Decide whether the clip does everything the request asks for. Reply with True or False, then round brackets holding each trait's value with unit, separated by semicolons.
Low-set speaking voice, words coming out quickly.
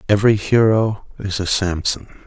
False (100 Hz; 130 wpm)